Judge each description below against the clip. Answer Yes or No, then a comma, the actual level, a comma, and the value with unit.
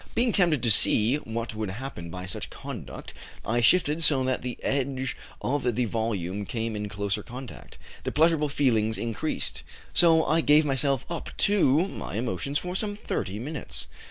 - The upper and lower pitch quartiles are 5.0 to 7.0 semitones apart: Yes, wide, 5.5 semitones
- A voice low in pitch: Yes, low, 130 Hz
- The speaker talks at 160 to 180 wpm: Yes, average, 165 wpm